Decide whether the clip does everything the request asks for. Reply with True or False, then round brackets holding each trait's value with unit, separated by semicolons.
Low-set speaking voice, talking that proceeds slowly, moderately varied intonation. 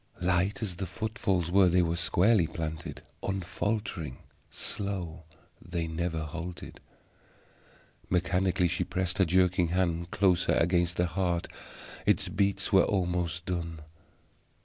False (90 Hz; 120 wpm; 1.9 semitones)